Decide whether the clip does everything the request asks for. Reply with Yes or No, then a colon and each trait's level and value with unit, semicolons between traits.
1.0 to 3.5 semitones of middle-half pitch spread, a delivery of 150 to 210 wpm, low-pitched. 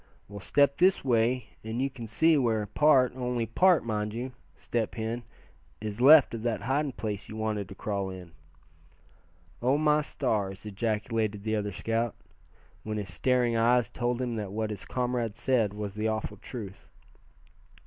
Yes: average, 3.1 semitones; average, 165 wpm; low, 115 Hz